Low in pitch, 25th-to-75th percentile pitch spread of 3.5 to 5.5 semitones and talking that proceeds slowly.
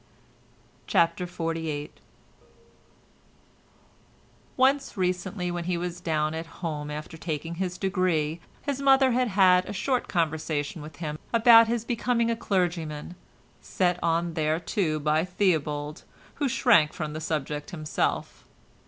No: medium, 170 Hz; average, 3.9 semitones; slow, 125 wpm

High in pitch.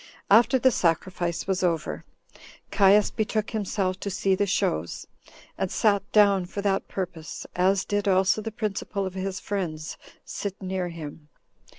Yes: high, 195 Hz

